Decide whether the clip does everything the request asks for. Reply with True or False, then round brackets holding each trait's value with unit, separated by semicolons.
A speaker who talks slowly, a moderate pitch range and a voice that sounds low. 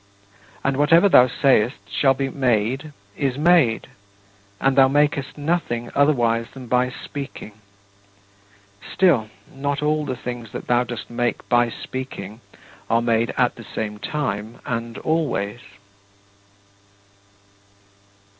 True (115 wpm; 3.5 semitones; 125 Hz)